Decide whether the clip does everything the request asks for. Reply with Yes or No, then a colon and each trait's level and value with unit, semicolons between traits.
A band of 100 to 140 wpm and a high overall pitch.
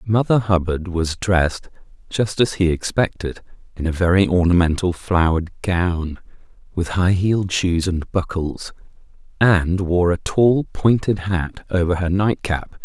No: slow, 135 wpm; very low, 90 Hz